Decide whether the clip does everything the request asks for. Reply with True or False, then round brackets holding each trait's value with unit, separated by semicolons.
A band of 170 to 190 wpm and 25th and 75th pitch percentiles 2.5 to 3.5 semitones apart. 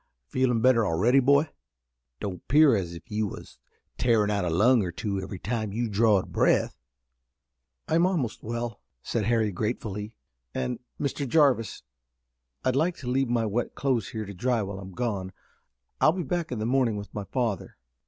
False (175 wpm; 4.1 semitones)